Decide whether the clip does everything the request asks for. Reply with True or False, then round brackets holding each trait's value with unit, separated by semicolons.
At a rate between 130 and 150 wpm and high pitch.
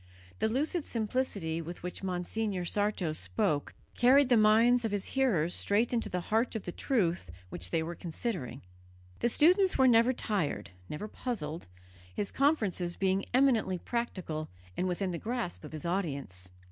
False (160 wpm; 200 Hz)